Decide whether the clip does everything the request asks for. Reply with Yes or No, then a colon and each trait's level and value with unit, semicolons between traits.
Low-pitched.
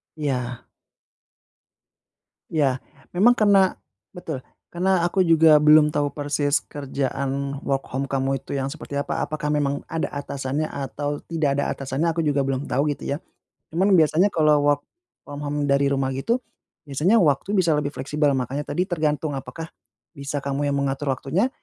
No: medium, 145 Hz